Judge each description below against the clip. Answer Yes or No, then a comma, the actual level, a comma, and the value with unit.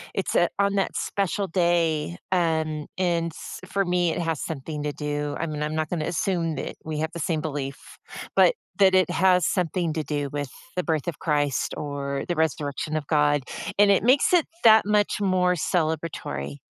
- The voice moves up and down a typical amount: Yes, average, 3.4 semitones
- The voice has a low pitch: No, medium, 160 Hz